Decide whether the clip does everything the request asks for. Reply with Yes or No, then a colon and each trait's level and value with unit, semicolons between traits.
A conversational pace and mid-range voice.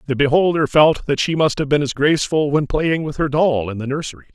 No: fast, 250 wpm; medium, 145 Hz